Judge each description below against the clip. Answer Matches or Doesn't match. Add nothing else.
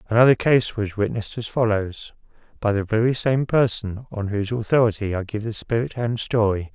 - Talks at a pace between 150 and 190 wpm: Matches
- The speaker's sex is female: Doesn't match